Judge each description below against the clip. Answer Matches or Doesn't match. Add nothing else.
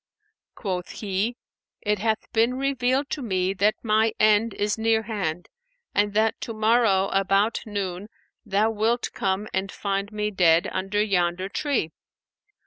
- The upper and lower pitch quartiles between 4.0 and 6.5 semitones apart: Doesn't match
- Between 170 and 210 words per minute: Doesn't match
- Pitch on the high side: Matches